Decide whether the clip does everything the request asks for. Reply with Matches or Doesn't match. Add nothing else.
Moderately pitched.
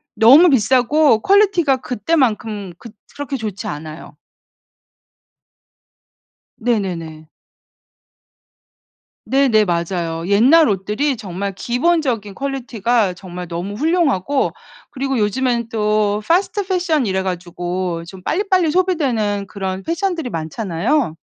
Doesn't match